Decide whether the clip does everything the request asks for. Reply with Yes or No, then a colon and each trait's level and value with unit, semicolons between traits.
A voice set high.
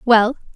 Yes: high, 230 Hz